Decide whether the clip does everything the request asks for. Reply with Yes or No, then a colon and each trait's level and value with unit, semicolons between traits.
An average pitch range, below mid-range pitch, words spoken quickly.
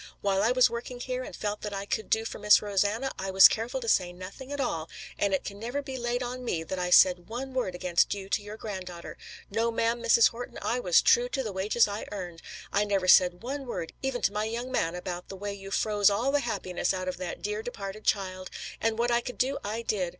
No: average, 4.1 semitones; high, 210 Hz; fast, 245 wpm